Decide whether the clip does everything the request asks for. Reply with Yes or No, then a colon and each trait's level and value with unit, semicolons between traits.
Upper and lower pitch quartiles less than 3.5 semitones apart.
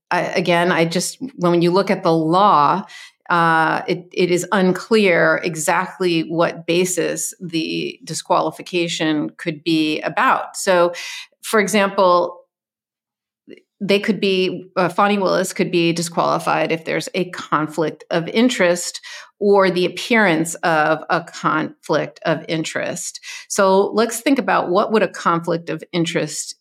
Yes: average, 3.0 semitones